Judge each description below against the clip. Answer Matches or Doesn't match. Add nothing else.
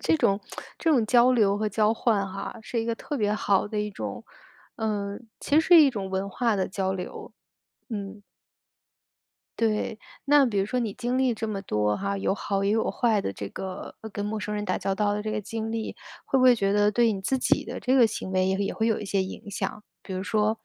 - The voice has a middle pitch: Doesn't match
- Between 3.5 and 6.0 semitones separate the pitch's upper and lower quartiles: Doesn't match